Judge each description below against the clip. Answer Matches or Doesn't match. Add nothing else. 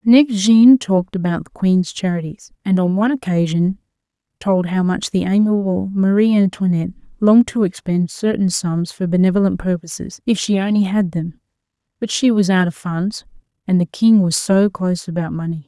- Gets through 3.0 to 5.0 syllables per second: Doesn't match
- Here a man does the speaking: Doesn't match